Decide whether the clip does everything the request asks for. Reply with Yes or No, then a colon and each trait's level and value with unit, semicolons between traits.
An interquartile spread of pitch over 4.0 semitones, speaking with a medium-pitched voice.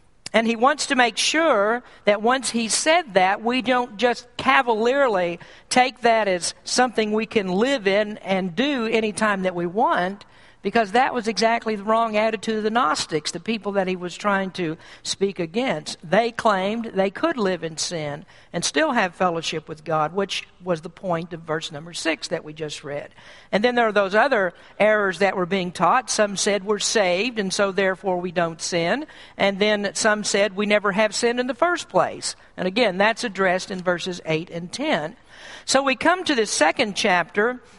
No: average, 4.5 semitones; high, 205 Hz